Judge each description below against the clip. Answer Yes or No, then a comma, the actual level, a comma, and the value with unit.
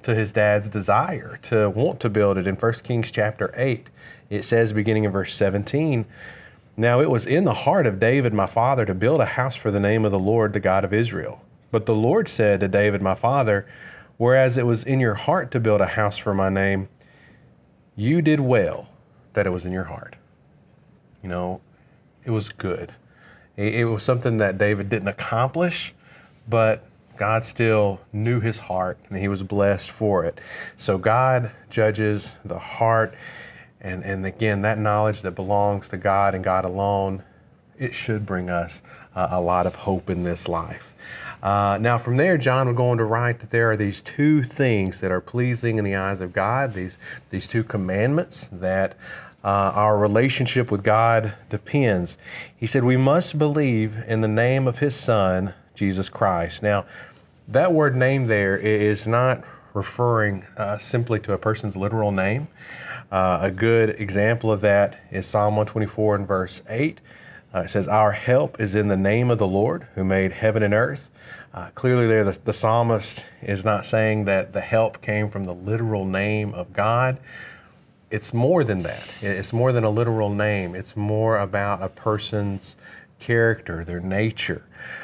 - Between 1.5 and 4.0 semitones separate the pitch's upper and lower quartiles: Yes, average, 2.9 semitones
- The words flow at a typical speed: Yes, average, 180 wpm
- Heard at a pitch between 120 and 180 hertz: No, low, 105 Hz